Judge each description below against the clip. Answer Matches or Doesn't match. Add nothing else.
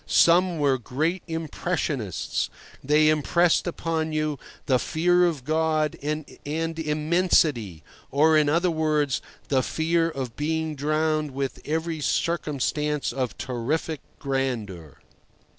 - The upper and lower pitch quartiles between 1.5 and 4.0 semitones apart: Matches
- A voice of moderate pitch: Matches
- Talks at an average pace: Doesn't match